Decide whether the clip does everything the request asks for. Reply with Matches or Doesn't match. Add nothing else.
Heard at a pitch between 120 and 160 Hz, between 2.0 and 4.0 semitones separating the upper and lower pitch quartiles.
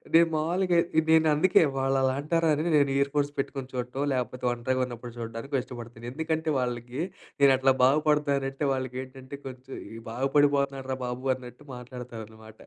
Matches